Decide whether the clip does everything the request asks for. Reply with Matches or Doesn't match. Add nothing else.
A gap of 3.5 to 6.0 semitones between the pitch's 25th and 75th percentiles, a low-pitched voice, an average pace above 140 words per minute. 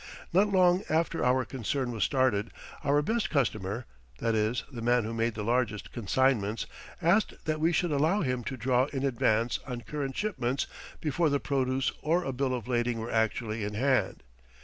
Matches